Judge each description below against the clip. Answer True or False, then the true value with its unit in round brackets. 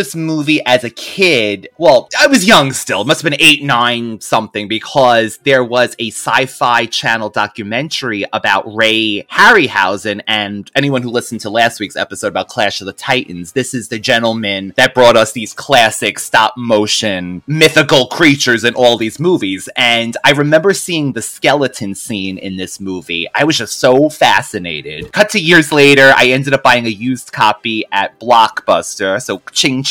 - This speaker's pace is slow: False (170 wpm)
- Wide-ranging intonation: False (4.9 semitones)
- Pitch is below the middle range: True (120 Hz)